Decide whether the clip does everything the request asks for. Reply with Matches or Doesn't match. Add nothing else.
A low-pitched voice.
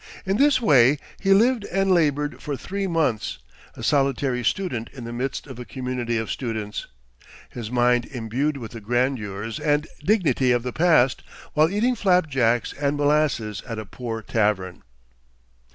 Matches